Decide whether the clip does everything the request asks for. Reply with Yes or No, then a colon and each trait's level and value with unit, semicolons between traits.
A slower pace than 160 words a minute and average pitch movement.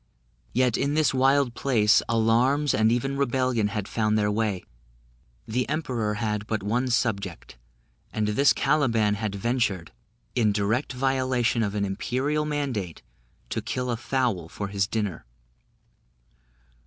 Yes: slow, 135 wpm; average, 3.9 semitones